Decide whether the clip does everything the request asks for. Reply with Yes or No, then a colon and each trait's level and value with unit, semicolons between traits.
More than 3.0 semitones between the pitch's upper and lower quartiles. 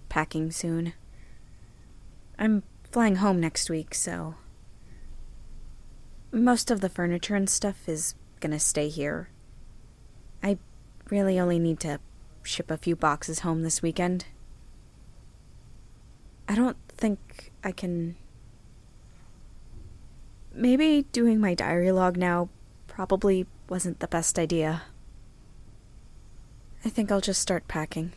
Yes: average, 4.3 semitones